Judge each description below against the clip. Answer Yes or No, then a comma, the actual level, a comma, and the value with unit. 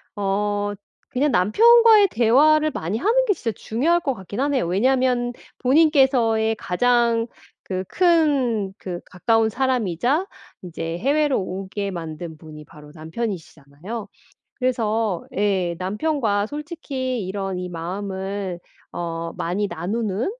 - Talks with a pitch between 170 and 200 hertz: No, high, 220 Hz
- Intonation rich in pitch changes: Yes, wide, 6.2 semitones